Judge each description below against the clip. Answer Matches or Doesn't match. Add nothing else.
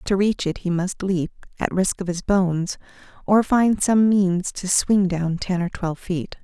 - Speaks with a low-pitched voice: Doesn't match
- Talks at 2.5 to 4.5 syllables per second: Matches